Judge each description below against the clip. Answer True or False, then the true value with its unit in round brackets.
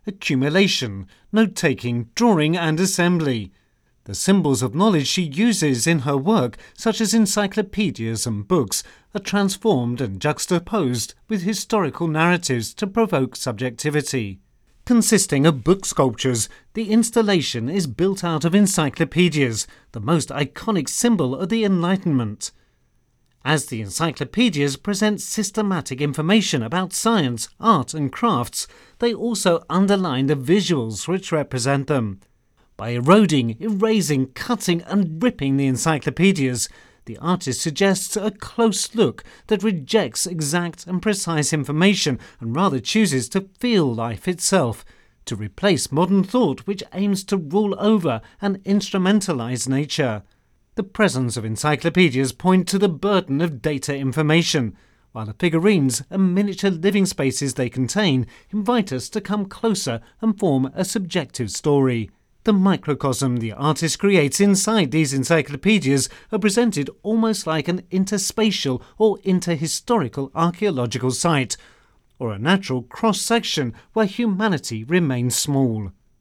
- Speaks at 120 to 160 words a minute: True (130 wpm)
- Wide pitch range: True (7.3 semitones)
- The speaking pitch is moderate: True (170 Hz)